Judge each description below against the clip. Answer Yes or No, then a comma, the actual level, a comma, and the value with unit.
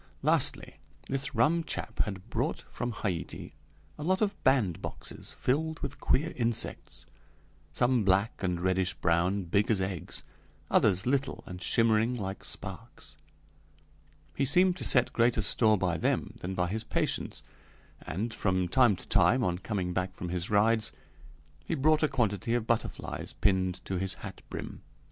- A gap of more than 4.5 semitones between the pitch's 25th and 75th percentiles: Yes, average, 5.2 semitones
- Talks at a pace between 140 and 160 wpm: Yes, average, 155 wpm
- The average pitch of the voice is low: Yes, low, 110 Hz